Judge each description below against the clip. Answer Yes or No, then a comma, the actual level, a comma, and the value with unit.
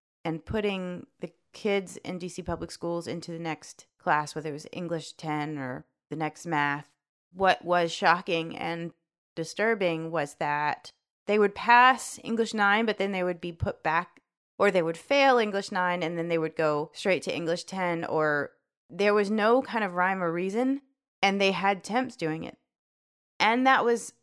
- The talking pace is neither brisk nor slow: Yes, average, 180 wpm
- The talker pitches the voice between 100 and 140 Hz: No, medium, 175 Hz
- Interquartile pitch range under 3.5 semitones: No, average, 4.2 semitones